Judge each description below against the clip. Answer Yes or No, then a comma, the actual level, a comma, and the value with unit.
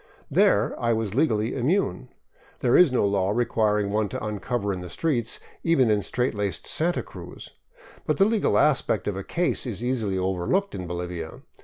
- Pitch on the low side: Yes, low, 110 Hz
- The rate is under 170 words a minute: No, average, 175 wpm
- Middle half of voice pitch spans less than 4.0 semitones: No, average, 4.9 semitones